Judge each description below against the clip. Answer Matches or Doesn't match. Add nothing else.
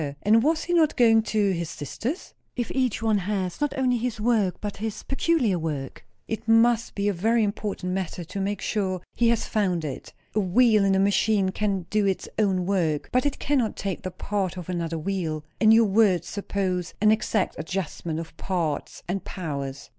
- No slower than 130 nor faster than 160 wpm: Doesn't match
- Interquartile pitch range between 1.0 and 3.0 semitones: Doesn't match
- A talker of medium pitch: Doesn't match